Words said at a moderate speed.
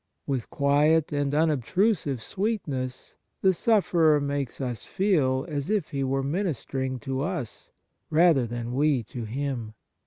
No: slow, 130 wpm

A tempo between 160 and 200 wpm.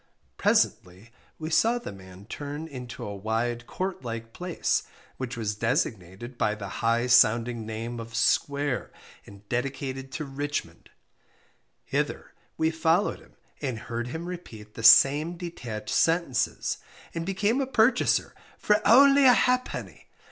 No: average, 140 wpm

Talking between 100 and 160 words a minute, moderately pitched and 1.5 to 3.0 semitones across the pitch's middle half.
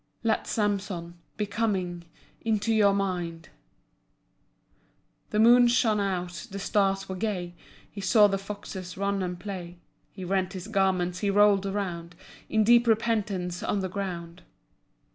No: average, 140 wpm; high, 195 Hz; narrow, 2.6 semitones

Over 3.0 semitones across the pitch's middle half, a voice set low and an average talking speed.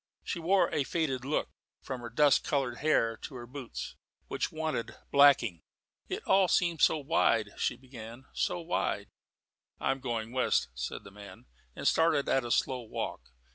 Yes: average, 4.8 semitones; low, 130 Hz; average, 170 wpm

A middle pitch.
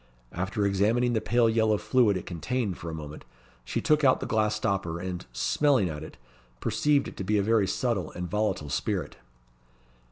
No: low, 100 Hz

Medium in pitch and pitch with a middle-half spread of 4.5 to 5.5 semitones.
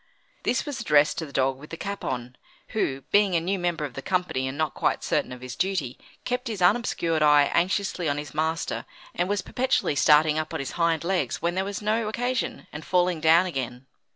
Yes: medium, 165 Hz; average, 4.9 semitones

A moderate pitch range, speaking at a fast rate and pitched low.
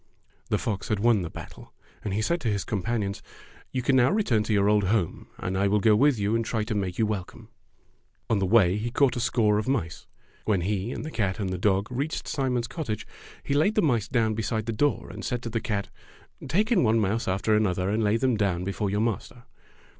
Yes: average, 3.3 semitones; fast, 235 wpm; low, 110 Hz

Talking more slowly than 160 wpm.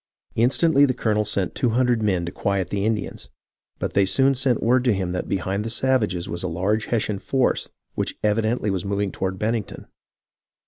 No: average, 185 wpm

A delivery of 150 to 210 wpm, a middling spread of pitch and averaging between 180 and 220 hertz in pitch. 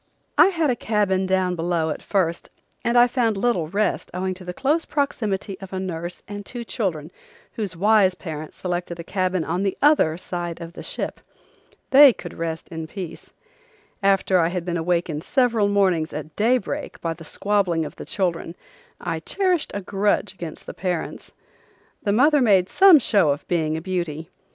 Yes: average, 180 wpm; average, 3.9 semitones; medium, 185 Hz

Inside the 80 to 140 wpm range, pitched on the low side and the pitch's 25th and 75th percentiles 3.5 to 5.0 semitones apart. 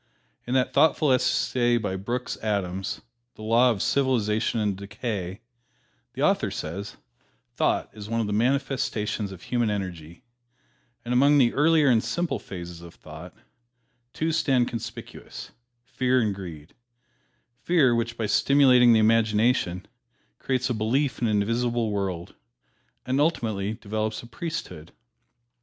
Yes: slow, 135 wpm; low, 115 Hz; average, 4.0 semitones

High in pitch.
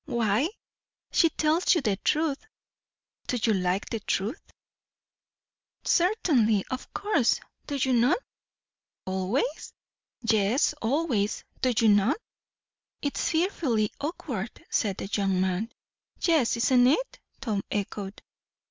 Yes: high, 235 Hz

